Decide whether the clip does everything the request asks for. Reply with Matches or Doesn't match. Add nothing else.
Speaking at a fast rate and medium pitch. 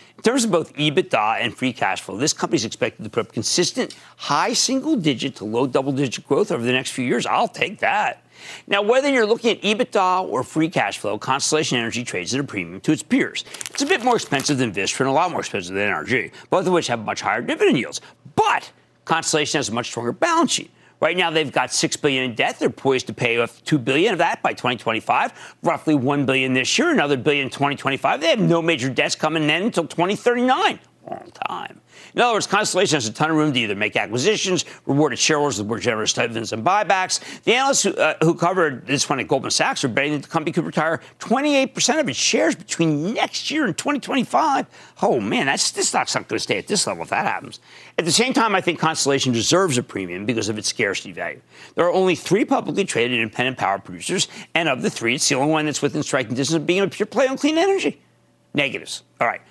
Matches